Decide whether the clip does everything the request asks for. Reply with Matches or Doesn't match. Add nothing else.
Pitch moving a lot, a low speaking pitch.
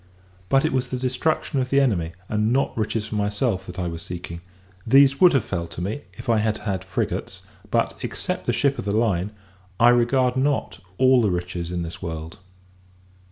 Matches